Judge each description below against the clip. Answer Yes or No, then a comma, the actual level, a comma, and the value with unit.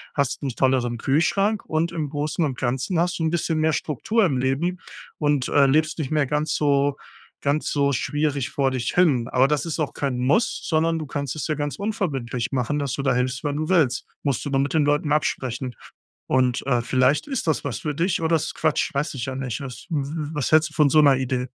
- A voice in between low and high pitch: Yes, medium, 145 Hz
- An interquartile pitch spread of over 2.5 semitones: Yes, average, 2.9 semitones